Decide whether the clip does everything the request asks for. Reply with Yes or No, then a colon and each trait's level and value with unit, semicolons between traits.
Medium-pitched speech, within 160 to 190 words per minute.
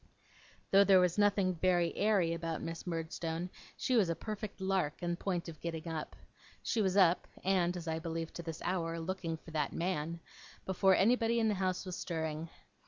Yes: medium, 175 Hz; average, 185 wpm